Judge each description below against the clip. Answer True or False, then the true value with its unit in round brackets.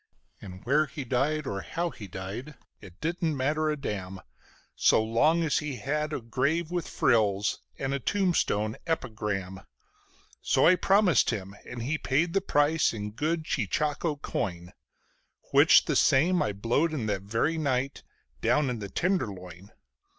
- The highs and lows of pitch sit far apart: True (6.9 semitones)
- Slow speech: False (155 wpm)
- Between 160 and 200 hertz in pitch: False (135 Hz)